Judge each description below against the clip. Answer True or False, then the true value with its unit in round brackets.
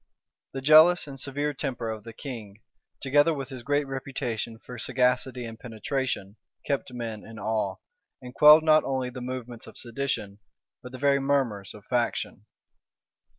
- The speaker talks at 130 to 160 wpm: True (155 wpm)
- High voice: False (125 Hz)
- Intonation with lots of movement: False (3.4 semitones)